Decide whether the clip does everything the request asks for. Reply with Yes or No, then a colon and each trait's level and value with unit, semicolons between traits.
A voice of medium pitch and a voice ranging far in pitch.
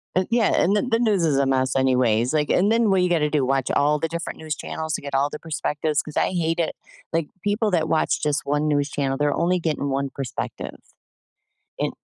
No: medium, 155 Hz; average, 3.6 semitones